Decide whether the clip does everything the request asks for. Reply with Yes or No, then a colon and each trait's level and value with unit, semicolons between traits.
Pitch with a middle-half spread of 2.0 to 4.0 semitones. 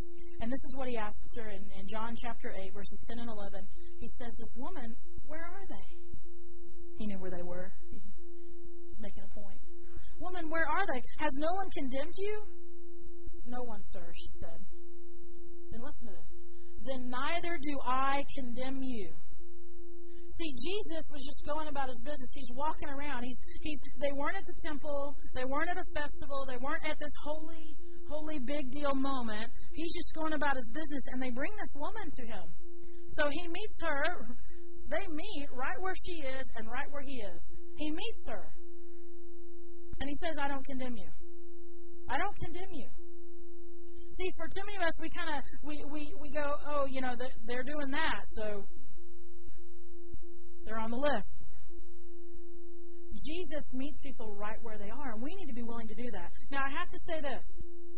No: average, 4.6 semitones